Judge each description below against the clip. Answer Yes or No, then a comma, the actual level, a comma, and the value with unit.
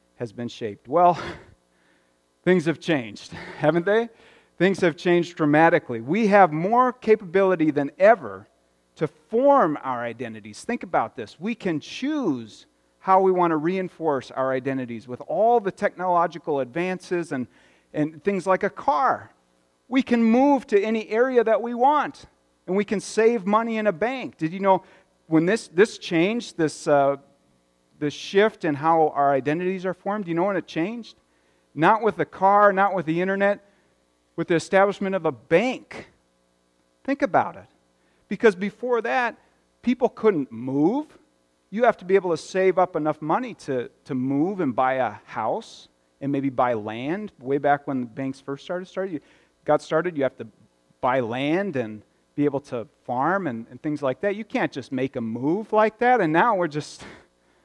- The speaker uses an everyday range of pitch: No, wide, 7.7 semitones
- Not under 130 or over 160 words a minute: No, average, 175 wpm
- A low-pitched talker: No, medium, 165 Hz